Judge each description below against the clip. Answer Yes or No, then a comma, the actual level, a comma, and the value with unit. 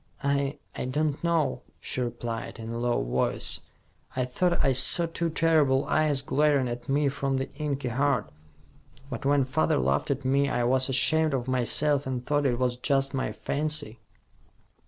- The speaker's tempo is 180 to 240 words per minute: No, average, 170 wpm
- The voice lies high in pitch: No, low, 135 Hz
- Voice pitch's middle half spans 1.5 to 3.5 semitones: Yes, average, 2.8 semitones